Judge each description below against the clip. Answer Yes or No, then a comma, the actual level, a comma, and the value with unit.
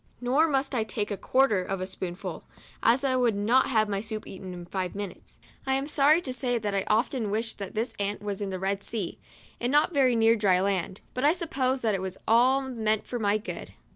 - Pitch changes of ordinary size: Yes, average, 4.5 semitones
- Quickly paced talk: Yes, fast, 230 wpm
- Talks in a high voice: Yes, high, 220 Hz